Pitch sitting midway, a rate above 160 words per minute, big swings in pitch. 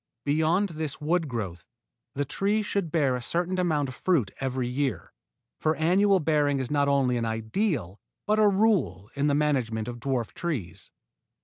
Yes: medium, 145 Hz; average, 170 wpm; wide, 5.9 semitones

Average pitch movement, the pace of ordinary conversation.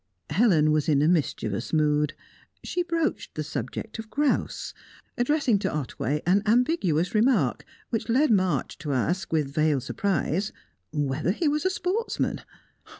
No: wide, 8.3 semitones; average, 145 wpm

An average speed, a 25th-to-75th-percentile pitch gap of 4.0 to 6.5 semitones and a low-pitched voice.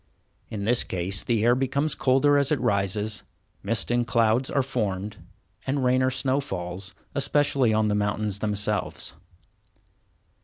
Yes: average, 145 wpm; average, 4.3 semitones; low, 115 Hz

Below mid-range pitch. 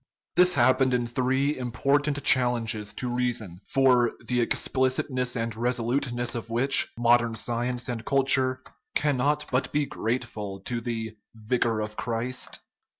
Yes: low, 125 Hz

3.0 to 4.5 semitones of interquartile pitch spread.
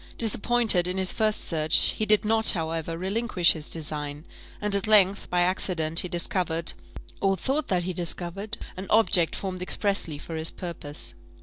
Yes: average, 3.9 semitones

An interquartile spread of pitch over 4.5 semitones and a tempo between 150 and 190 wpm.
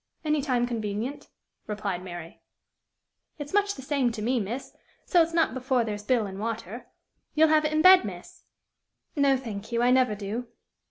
Yes: wide, 5.5 semitones; average, 170 wpm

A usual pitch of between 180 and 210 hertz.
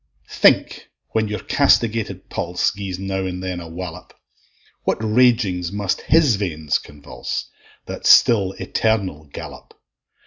No: very low, 95 Hz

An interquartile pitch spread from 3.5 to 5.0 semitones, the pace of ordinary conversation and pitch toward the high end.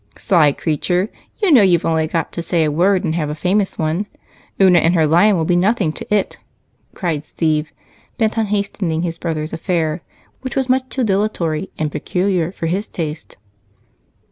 No: average, 4.0 semitones; average, 180 wpm; medium, 175 Hz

